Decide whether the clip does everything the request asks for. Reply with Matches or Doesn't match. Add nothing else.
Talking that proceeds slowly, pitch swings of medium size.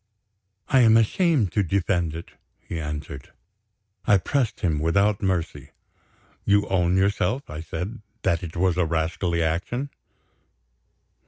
Matches